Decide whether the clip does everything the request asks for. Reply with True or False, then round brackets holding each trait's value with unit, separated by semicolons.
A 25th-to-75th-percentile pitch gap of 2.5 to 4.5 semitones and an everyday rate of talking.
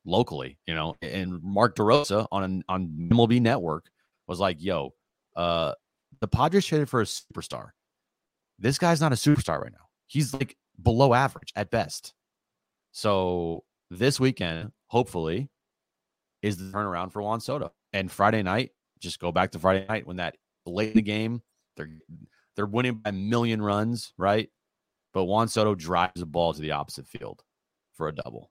False (5.2 semitones; 165 wpm)